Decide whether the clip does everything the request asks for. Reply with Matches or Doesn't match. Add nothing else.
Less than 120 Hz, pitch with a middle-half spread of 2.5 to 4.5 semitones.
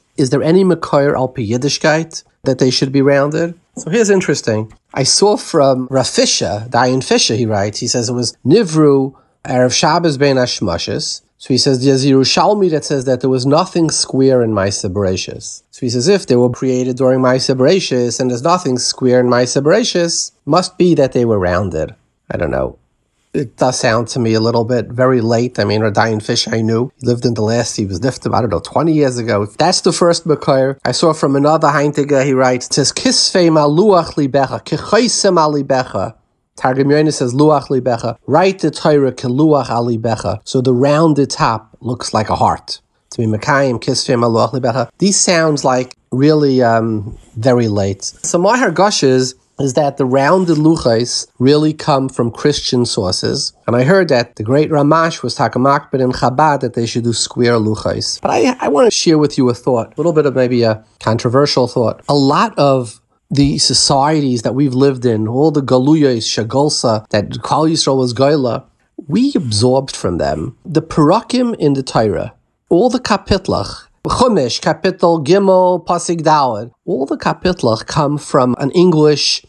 Doesn't match